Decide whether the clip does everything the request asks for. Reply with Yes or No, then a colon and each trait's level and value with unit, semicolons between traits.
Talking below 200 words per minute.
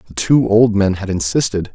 No: fast, 205 wpm